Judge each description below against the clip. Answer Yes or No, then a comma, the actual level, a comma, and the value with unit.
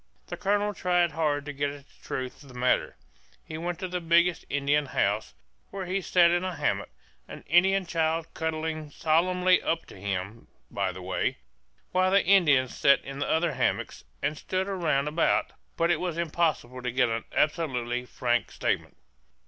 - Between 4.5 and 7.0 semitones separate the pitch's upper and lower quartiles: Yes, average, 5.2 semitones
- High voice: No, medium, 155 Hz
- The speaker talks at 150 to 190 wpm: Yes, average, 175 wpm